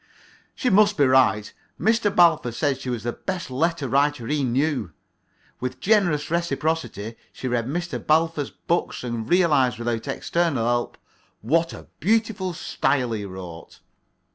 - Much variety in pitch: Yes, wide, 6.0 semitones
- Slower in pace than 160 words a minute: Yes, average, 140 wpm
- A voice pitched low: No, medium, 145 Hz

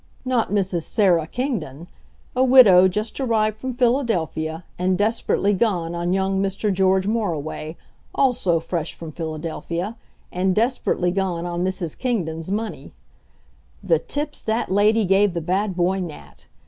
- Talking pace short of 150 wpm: Yes, slow, 135 wpm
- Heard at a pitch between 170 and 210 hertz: Yes, high, 190 Hz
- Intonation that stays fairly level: No, average, 4.3 semitones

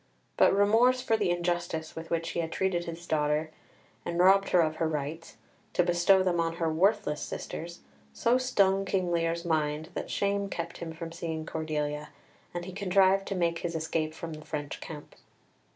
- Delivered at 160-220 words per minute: Yes, average, 185 wpm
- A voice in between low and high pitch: Yes, medium, 170 Hz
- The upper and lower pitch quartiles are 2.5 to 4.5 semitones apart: Yes, average, 2.9 semitones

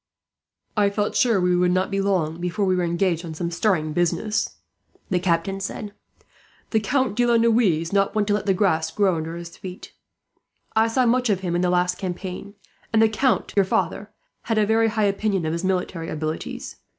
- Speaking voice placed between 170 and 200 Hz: Yes, high, 190 Hz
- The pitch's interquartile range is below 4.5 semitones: Yes, average, 3.5 semitones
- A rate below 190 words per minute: No, fast, 205 wpm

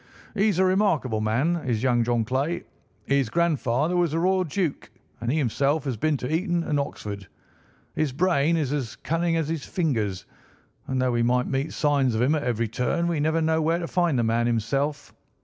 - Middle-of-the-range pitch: Yes, medium, 145 Hz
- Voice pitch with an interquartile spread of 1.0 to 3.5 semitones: No, average, 5.3 semitones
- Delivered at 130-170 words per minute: No, average, 195 wpm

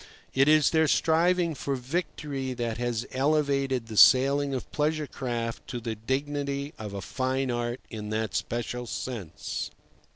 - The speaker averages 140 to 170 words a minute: Yes, average, 150 wpm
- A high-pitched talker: No, low, 130 Hz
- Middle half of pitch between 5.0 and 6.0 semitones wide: No, average, 3.3 semitones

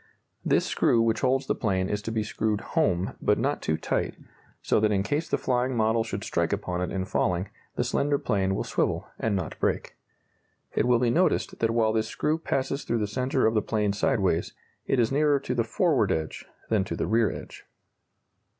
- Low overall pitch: Yes, low, 110 Hz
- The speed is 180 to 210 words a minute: Yes, fast, 205 wpm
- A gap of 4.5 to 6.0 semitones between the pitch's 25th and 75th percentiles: No, average, 4.1 semitones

